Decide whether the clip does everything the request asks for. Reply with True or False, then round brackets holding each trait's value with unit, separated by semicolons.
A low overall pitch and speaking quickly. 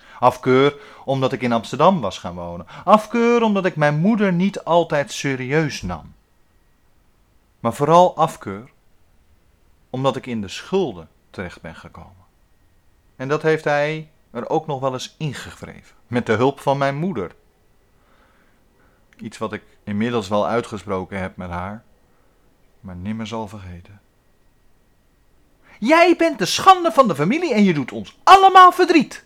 False (125 Hz; 145 wpm)